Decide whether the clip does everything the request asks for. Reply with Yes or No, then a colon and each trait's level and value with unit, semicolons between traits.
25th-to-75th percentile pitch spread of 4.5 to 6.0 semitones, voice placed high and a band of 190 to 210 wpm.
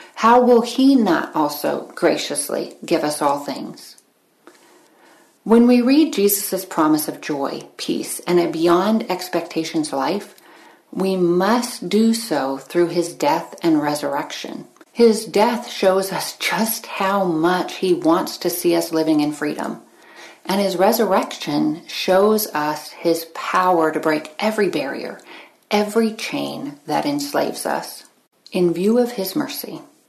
No: wide, 5.5 semitones; high, 195 Hz; slow, 135 wpm